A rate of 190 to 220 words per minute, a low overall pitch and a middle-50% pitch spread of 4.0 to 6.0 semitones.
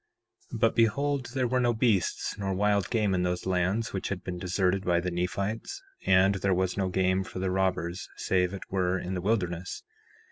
No: average, 200 wpm; very low, 95 Hz; narrow, 2.5 semitones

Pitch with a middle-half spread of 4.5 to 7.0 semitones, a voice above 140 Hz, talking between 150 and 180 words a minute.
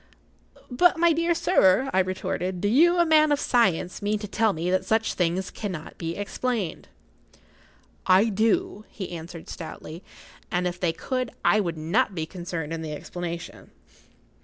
Yes: wide, 5.6 semitones; high, 190 Hz; average, 160 wpm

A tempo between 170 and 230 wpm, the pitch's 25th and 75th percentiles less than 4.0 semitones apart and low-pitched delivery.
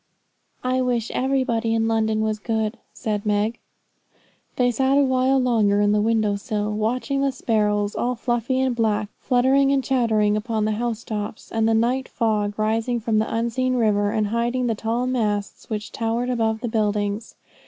No: average, 175 wpm; average, 2.7 semitones; high, 225 Hz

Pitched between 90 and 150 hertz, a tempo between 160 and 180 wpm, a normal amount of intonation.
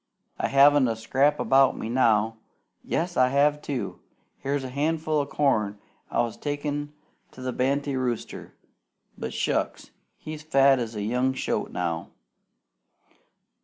No: low, 135 Hz; average, 140 wpm; average, 3.5 semitones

